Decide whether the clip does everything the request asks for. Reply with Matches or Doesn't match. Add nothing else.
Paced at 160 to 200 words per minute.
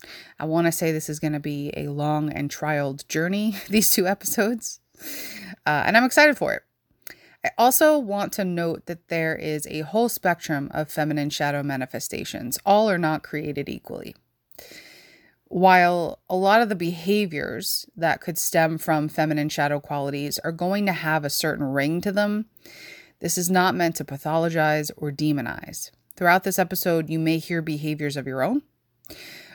Matches